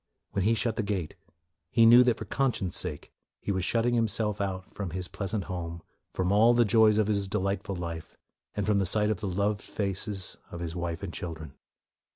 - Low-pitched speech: Yes, low, 100 Hz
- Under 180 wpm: No, average, 200 wpm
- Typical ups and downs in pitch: Yes, average, 3.0 semitones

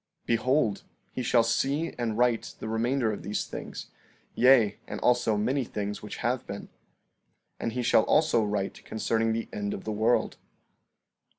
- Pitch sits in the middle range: No, low, 115 Hz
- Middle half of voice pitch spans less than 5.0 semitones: Yes, narrow, 2.6 semitones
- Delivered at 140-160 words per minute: No, average, 170 wpm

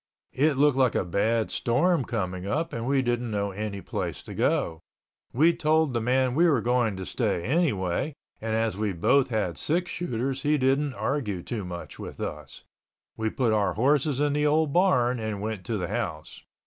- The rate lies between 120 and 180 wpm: No, average, 190 wpm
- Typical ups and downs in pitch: No, wide, 5.8 semitones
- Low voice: Yes, low, 120 Hz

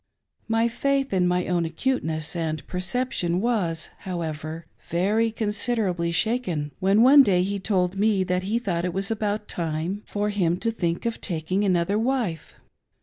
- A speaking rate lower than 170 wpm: Yes, average, 155 wpm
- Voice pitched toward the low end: No, high, 190 Hz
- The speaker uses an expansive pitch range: No, average, 4.6 semitones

